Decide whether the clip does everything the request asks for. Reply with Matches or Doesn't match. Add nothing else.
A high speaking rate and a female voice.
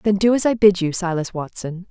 Matches